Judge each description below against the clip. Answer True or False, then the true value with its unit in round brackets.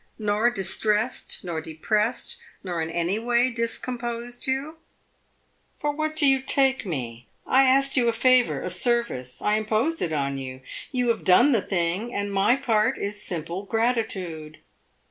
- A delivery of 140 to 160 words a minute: True (155 wpm)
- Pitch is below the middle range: False (220 Hz)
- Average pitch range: False (5.9 semitones)